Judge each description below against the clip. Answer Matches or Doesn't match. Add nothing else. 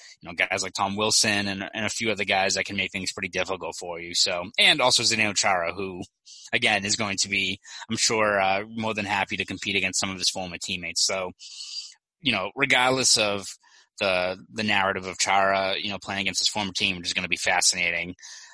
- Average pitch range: Doesn't match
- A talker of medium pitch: Doesn't match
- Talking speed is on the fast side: Matches